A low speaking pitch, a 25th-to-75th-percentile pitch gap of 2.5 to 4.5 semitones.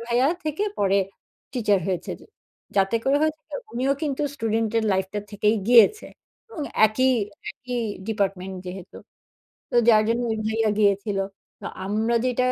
No: high, 225 Hz; average, 4.0 semitones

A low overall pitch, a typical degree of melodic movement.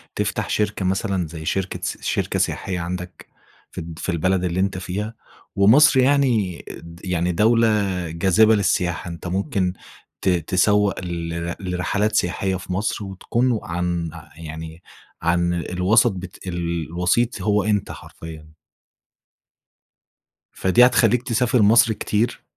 Yes: very low, 95 Hz; average, 3.5 semitones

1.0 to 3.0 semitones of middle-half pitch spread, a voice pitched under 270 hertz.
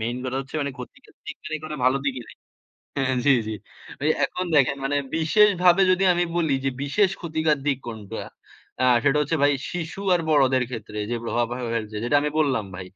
No: average, 4.2 semitones; medium, 140 Hz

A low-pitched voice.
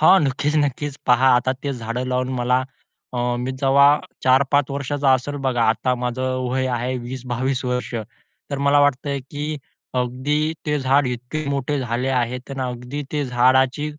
Yes: low, 130 Hz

